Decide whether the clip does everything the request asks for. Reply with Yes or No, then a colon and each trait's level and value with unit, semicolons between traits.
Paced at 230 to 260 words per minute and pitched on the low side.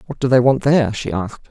No: fast, 280 wpm; low, 125 Hz